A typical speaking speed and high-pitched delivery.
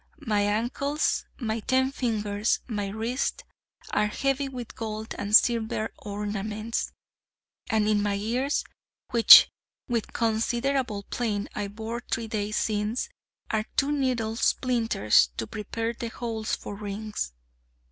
No: slow, 125 wpm; high, 220 Hz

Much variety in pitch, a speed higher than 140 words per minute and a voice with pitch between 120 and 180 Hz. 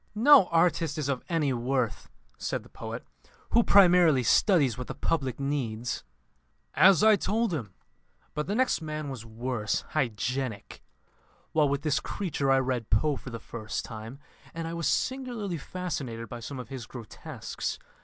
Yes: wide, 5.7 semitones; average, 160 wpm; medium, 140 Hz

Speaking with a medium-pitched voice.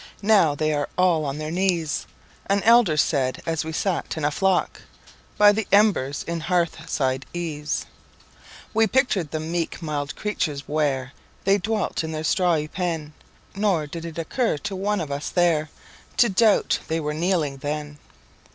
Yes: medium, 165 Hz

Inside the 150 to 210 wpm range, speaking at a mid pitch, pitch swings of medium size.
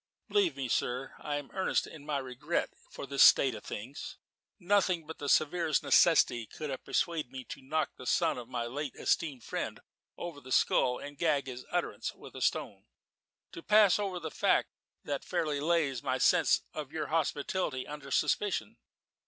Yes: average, 180 wpm; medium, 145 Hz; average, 4.1 semitones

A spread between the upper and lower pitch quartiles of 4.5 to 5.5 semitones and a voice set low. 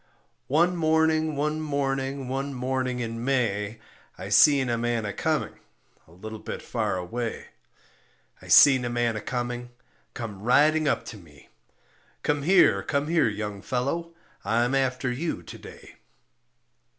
No: average, 4.0 semitones; low, 125 Hz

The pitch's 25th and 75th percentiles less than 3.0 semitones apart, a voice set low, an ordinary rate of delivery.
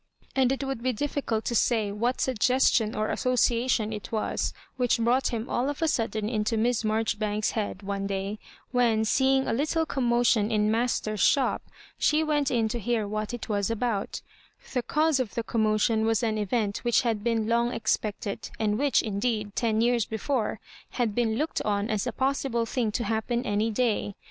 No: narrow, 2.6 semitones; high, 230 Hz; average, 190 wpm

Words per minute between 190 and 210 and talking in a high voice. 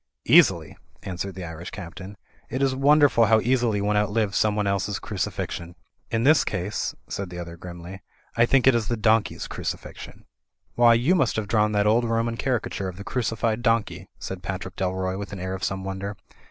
No: average, 195 wpm; low, 105 Hz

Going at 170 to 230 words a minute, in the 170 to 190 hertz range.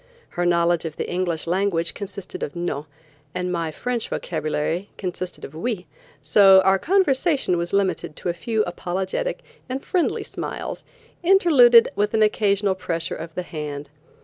No: average, 150 wpm; medium, 185 Hz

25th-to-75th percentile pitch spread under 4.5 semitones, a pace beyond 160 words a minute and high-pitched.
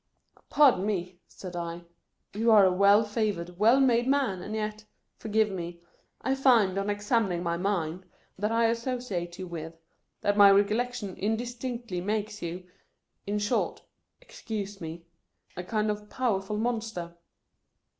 Yes: average, 3.8 semitones; average, 170 wpm; high, 205 Hz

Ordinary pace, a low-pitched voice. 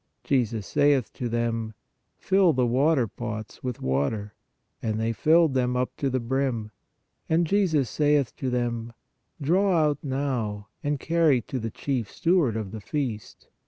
Yes: average, 150 wpm; low, 125 Hz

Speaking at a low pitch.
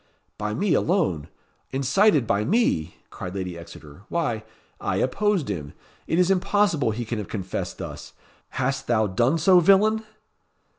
Yes: low, 130 Hz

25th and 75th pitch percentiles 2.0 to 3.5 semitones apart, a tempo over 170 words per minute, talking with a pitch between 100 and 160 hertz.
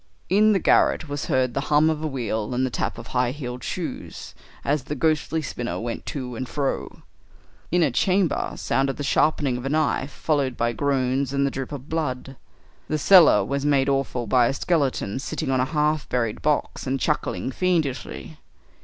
Yes: average, 3.1 semitones; average, 190 wpm; medium, 140 Hz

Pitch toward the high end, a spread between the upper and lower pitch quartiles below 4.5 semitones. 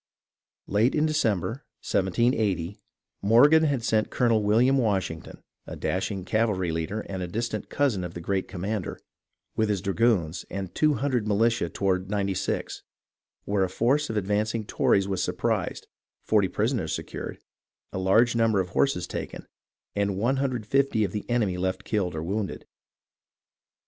No: low, 105 Hz; average, 3.7 semitones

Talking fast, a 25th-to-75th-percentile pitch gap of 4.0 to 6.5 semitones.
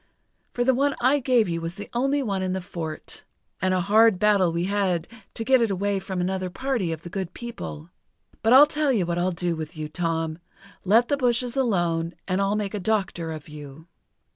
Yes: fast, 215 wpm; wide, 5.5 semitones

